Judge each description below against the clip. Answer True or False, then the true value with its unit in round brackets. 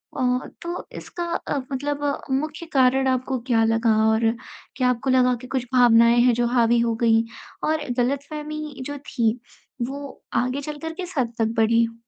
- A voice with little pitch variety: False (3.6 semitones)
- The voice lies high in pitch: True (255 Hz)